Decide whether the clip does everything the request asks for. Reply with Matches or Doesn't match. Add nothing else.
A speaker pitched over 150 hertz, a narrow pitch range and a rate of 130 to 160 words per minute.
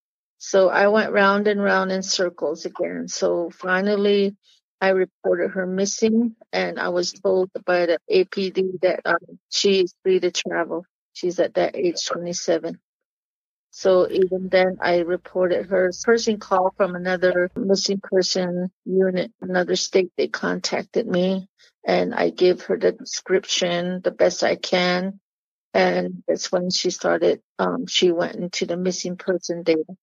Matches